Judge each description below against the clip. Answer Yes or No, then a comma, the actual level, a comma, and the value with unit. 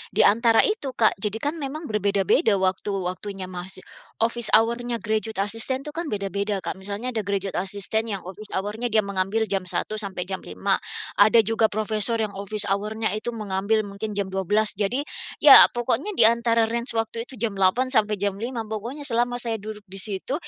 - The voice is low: No, high, 215 Hz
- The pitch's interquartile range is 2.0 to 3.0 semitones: Yes, average, 2.7 semitones